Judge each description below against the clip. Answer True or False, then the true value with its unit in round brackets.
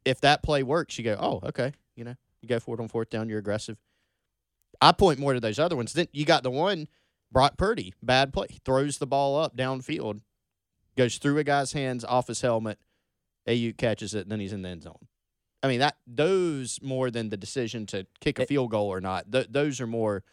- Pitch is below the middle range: True (120 Hz)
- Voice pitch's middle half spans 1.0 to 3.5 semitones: False (4.5 semitones)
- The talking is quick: True (225 wpm)